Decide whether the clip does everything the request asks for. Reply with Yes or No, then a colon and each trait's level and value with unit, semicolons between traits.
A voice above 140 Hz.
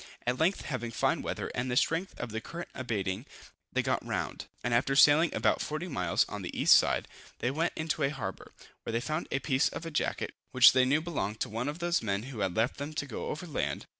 No: low, 135 Hz